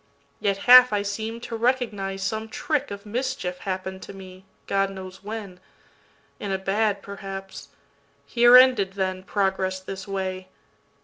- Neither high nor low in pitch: No, high, 195 Hz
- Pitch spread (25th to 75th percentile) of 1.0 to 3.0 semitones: Yes, average, 2.7 semitones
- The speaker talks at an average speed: No, slow, 125 wpm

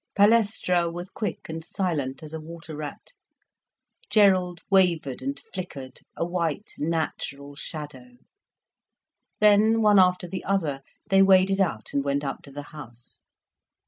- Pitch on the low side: No, medium, 170 Hz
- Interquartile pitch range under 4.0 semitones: No, average, 4.9 semitones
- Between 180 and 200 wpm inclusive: No, slow, 135 wpm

